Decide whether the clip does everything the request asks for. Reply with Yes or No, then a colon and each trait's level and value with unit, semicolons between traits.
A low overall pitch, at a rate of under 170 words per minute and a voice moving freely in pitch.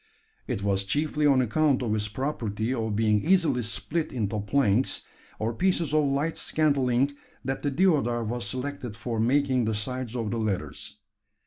No: low, 125 Hz; average, 160 wpm; average, 4.6 semitones